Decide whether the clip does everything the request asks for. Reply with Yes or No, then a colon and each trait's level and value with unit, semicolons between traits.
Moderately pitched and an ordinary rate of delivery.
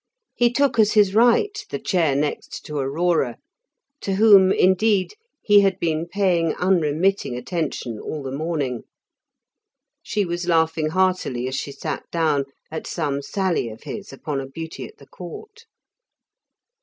Yes: medium, 170 Hz; average, 145 wpm